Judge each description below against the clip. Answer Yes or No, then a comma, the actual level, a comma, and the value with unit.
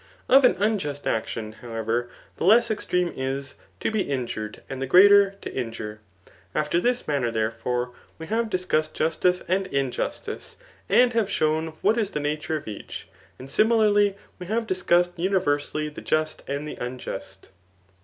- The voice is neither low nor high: Yes, medium, 155 Hz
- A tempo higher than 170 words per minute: No, average, 165 wpm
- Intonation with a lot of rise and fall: Yes, wide, 7.4 semitones